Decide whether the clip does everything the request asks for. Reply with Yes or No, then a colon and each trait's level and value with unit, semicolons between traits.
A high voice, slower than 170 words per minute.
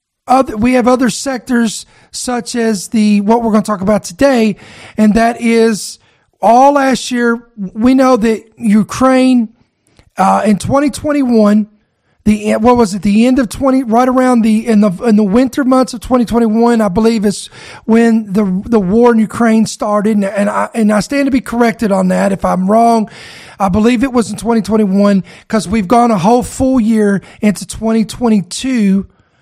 No: high, 225 Hz; average, 175 wpm